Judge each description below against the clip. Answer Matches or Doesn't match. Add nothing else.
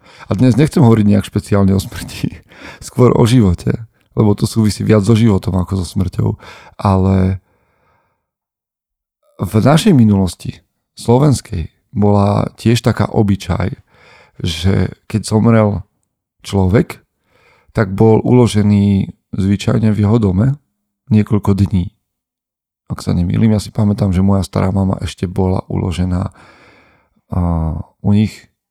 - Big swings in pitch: Doesn't match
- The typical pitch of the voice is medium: Doesn't match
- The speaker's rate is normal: Matches